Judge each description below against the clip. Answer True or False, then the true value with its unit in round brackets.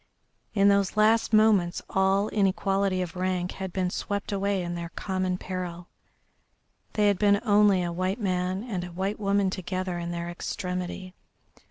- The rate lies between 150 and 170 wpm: True (160 wpm)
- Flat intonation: True (1.8 semitones)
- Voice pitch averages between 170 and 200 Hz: True (190 Hz)